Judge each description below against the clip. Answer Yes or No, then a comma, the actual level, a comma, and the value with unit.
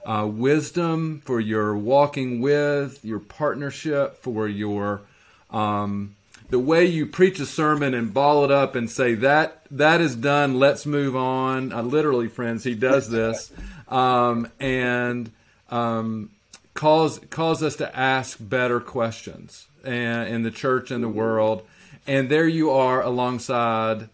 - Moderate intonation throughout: Yes, average, 4.0 semitones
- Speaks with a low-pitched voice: Yes, low, 130 Hz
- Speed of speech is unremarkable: Yes, average, 145 wpm